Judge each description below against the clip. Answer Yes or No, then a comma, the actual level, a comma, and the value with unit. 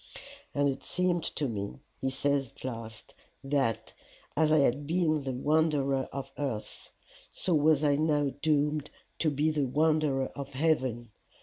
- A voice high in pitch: No, medium, 145 Hz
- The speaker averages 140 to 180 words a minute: Yes, average, 150 wpm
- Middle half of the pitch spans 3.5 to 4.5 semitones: No, narrow, 2.6 semitones